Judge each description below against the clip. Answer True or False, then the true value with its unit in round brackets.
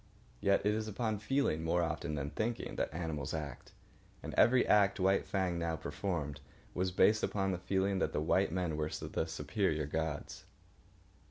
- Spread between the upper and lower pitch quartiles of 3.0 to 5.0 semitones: True (4.1 semitones)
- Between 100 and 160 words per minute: False (170 wpm)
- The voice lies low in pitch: True (90 Hz)